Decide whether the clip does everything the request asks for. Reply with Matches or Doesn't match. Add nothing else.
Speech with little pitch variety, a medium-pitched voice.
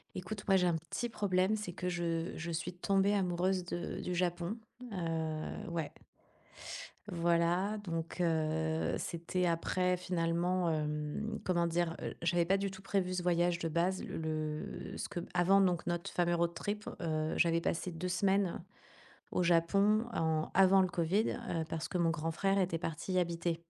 Matches